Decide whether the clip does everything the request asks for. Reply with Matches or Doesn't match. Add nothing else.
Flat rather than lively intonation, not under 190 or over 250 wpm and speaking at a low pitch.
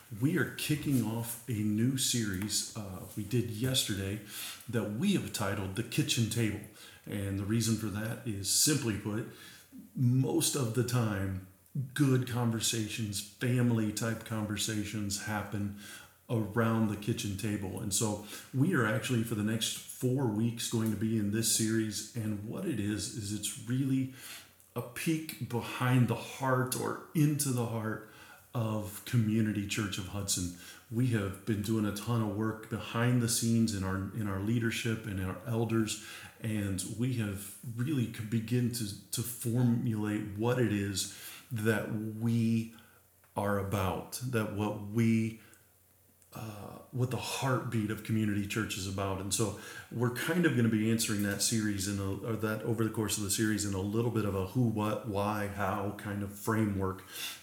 Doesn't match